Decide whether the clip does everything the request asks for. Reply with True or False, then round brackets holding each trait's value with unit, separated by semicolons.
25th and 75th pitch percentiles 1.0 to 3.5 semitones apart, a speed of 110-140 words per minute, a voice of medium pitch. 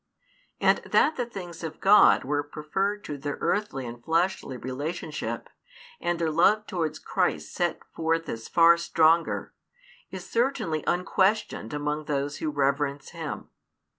False (4.3 semitones; 135 wpm; 160 Hz)